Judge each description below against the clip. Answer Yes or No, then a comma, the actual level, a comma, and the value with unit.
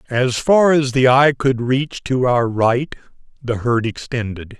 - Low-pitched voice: Yes, low, 125 Hz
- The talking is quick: No, average, 170 wpm